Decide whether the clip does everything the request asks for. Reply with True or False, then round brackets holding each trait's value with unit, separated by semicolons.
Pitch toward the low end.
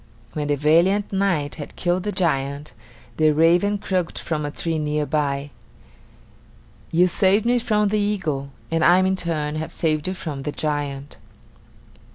False (160 Hz)